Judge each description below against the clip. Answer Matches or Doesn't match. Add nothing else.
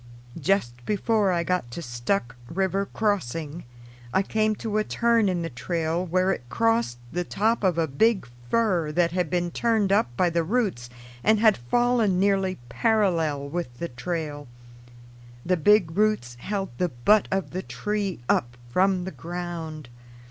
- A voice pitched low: Doesn't match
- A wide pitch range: Doesn't match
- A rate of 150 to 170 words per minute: Matches